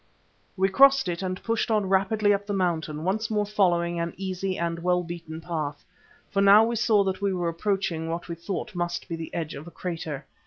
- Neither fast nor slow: No, fast, 210 wpm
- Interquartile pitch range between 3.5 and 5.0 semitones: No, average, 3.1 semitones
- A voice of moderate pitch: Yes, medium, 180 Hz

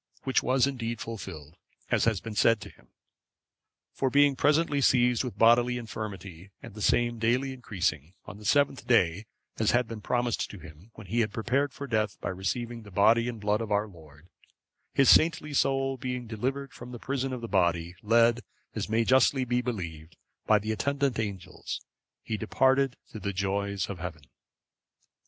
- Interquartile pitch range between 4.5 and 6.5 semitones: No, average, 4.0 semitones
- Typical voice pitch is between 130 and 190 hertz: No, low, 115 Hz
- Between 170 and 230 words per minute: Yes, average, 180 wpm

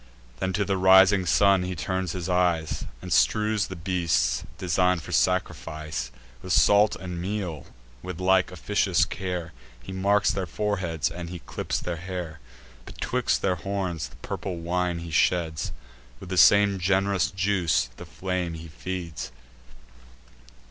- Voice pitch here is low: Yes, very low, 90 Hz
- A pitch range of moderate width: No, narrow, 2.2 semitones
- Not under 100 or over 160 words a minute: Yes, average, 145 wpm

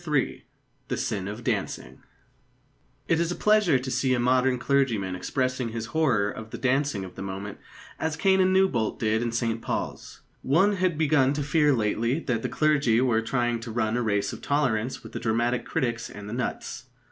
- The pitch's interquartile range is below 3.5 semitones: No, average, 4.5 semitones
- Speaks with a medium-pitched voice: No, low, 125 Hz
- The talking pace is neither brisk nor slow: Yes, average, 190 wpm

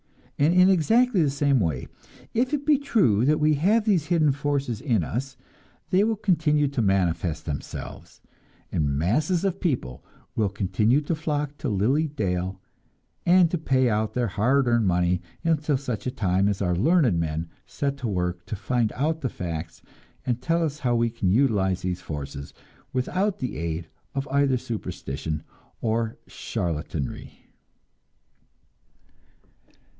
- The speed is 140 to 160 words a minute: Yes, average, 150 wpm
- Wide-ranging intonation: Yes, wide, 8.8 semitones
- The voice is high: No, low, 125 Hz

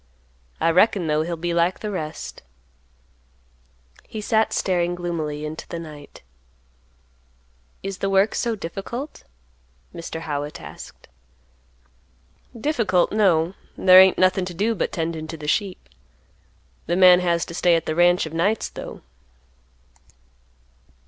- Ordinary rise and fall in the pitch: Yes, average, 3.0 semitones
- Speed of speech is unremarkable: No, slow, 130 wpm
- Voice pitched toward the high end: No, medium, 175 Hz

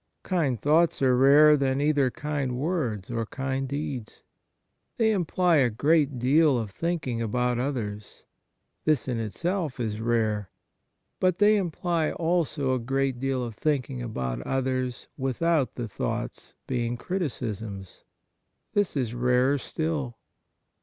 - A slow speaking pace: Yes, slow, 130 wpm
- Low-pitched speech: Yes, low, 130 Hz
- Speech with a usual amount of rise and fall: Yes, average, 4.4 semitones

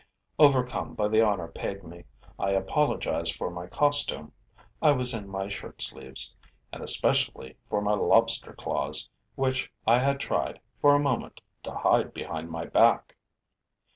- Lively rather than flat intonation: Yes, wide, 7.2 semitones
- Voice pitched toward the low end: Yes, low, 105 Hz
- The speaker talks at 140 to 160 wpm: Yes, average, 150 wpm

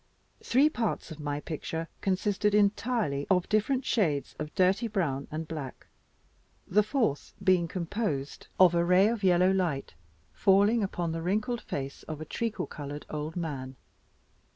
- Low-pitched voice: No, medium, 180 Hz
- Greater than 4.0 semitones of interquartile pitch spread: Yes, wide, 5.4 semitones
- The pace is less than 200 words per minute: Yes, average, 150 wpm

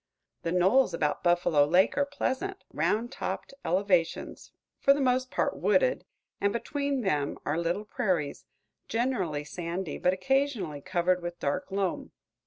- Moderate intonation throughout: No, wide, 7.1 semitones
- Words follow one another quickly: No, average, 140 wpm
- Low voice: No, medium, 185 Hz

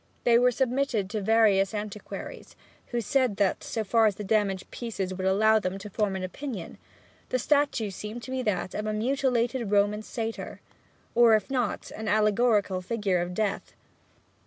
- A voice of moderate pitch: No, high, 215 Hz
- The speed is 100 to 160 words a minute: No, average, 170 wpm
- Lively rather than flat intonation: No, average, 3.2 semitones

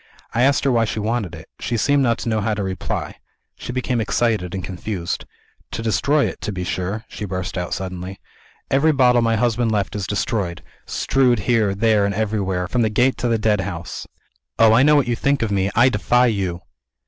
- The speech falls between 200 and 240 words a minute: Yes, fast, 205 wpm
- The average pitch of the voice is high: No, low, 110 Hz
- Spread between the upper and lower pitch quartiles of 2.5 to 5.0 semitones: Yes, average, 4.0 semitones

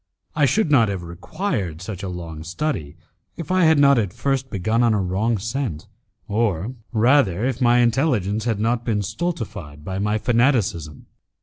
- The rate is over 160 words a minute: Yes, average, 170 wpm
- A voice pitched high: No, low, 110 Hz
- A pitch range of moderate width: No, wide, 5.9 semitones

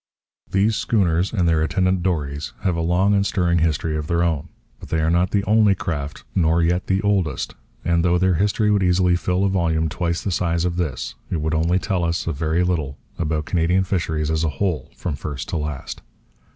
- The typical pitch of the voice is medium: No, very low, 85 Hz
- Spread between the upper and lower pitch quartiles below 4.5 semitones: Yes, average, 2.8 semitones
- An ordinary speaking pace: No, fast, 210 wpm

